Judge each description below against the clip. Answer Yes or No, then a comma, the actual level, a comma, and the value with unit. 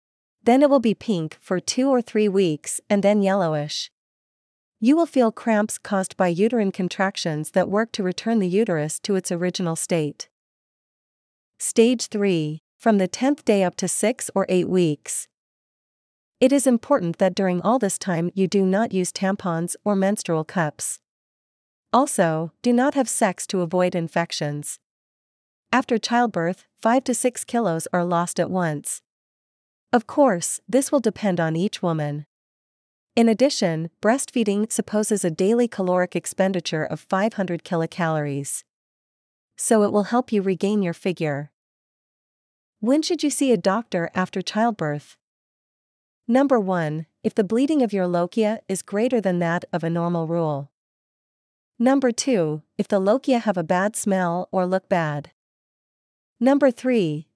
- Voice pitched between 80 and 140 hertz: No, high, 195 Hz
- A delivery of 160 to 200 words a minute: No, average, 150 wpm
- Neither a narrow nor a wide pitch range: Yes, average, 4.9 semitones